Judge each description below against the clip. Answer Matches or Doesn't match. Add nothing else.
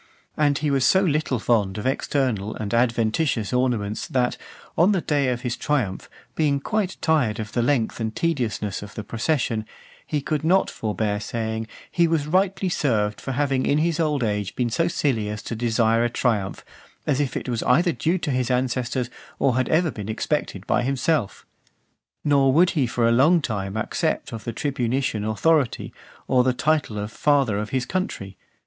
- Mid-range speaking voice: Doesn't match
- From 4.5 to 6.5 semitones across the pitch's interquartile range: Matches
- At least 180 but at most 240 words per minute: Matches